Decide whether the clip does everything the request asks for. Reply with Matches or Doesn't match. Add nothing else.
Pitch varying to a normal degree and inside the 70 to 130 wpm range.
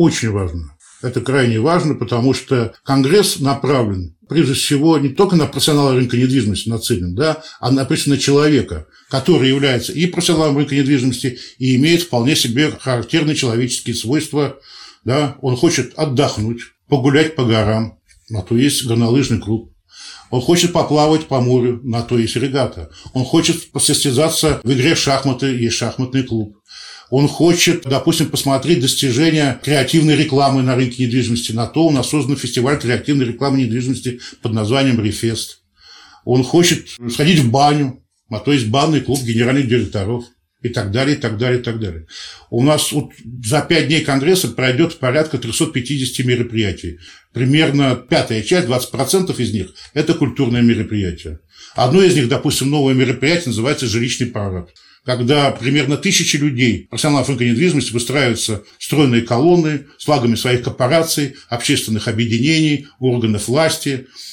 Doesn't match